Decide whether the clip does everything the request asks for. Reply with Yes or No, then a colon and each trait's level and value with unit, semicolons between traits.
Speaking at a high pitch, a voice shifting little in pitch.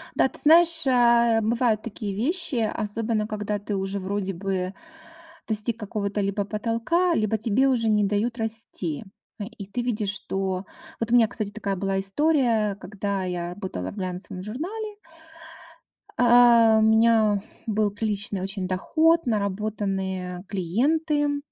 No: high, 215 Hz; average, 3.2 semitones